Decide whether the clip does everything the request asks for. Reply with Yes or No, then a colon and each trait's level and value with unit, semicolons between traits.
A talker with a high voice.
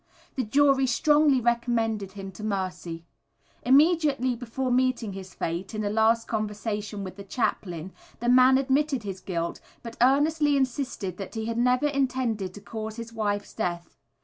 Yes: high, 230 Hz